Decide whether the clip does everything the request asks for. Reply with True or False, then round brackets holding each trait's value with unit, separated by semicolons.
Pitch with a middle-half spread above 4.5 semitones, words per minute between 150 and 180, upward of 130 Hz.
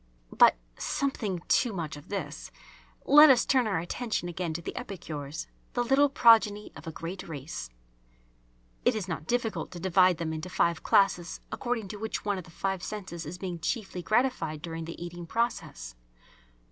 True (5.0 semitones; 170 wpm; 185 Hz)